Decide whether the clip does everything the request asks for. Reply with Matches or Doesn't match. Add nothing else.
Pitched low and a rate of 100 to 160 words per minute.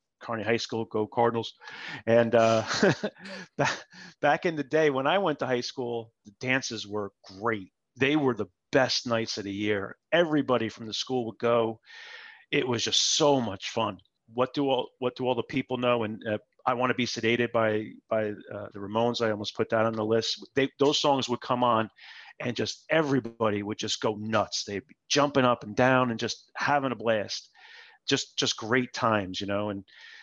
Doesn't match